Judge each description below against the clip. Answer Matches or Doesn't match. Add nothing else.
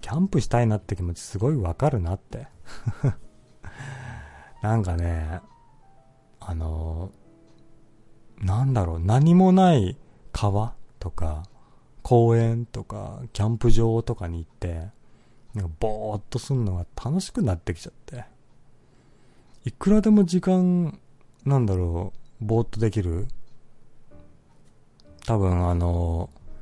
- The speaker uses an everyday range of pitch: Doesn't match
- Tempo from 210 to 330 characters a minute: Matches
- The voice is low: Matches